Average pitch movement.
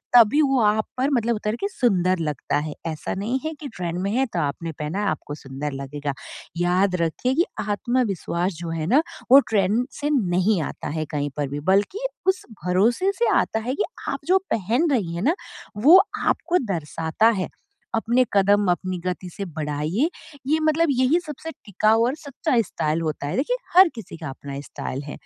No: wide, 7.8 semitones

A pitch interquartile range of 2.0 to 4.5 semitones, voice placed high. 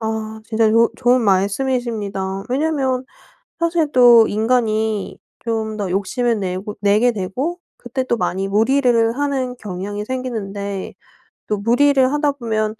Yes: average, 3.8 semitones; high, 225 Hz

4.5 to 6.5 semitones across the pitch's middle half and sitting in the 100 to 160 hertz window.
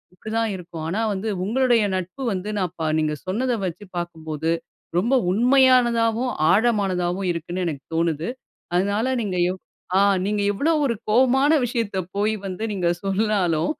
No: average, 4.9 semitones; high, 200 Hz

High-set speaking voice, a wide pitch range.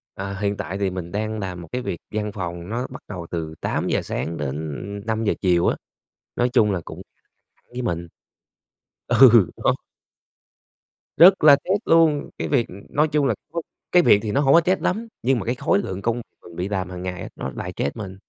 No: low, 105 Hz; wide, 6.2 semitones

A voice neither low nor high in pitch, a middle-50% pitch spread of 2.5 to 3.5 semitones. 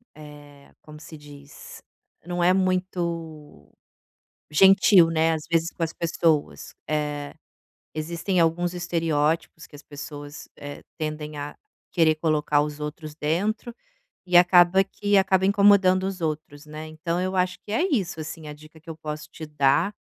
Yes: medium, 160 Hz; average, 3.1 semitones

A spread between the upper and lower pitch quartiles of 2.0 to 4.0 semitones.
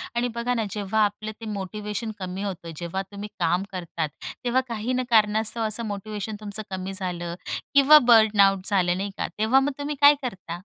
Yes: average, 3.3 semitones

